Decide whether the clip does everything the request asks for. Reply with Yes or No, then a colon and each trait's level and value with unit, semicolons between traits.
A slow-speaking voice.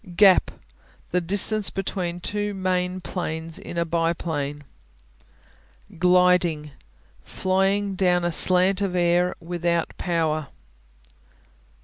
Yes: slow, 95 wpm